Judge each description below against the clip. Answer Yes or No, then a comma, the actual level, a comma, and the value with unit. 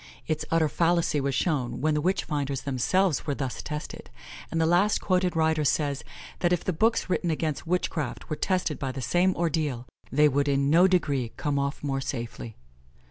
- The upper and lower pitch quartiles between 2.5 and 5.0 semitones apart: Yes, average, 3.8 semitones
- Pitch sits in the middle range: Yes, medium, 150 Hz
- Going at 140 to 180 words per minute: No, average, 190 wpm